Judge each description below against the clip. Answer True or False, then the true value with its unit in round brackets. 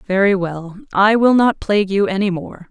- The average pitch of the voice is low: False (200 Hz)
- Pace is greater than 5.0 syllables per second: False (4.9 syllables/s)